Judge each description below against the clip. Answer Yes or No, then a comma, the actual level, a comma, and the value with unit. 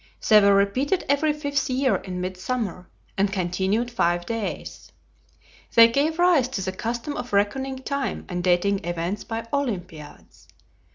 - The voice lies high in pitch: Yes, high, 215 Hz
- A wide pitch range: Yes, wide, 6.2 semitones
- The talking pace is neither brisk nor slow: Yes, average, 150 wpm